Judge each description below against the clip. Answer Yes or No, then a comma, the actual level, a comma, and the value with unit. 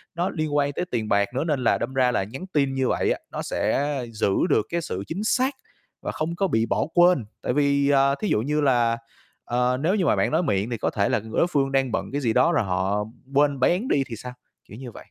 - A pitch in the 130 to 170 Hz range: Yes, low, 135 Hz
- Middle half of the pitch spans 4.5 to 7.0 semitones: Yes, average, 5.1 semitones